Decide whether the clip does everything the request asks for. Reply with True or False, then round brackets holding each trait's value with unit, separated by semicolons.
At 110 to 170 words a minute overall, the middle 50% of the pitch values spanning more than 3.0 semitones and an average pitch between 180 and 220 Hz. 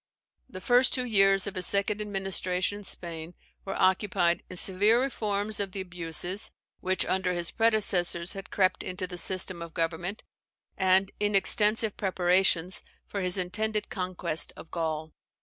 False (150 wpm; 2.4 semitones; 190 Hz)